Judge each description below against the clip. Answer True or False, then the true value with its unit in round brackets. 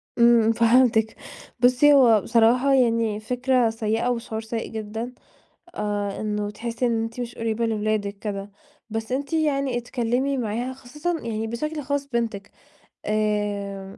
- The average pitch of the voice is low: False (230 Hz)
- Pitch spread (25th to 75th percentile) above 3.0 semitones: False (2.6 semitones)